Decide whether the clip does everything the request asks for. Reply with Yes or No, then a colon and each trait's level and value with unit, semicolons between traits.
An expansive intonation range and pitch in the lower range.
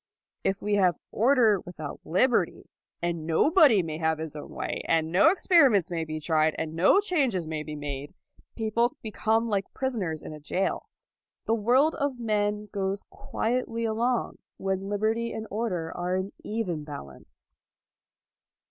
No: wide, 6.1 semitones; high, 200 Hz